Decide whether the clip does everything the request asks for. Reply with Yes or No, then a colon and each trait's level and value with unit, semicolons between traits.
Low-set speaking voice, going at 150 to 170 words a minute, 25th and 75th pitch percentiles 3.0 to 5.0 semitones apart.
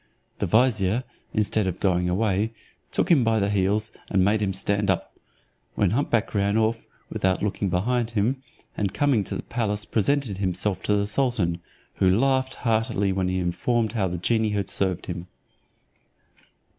Yes: low, 105 Hz; average, 165 wpm; average, 3.3 semitones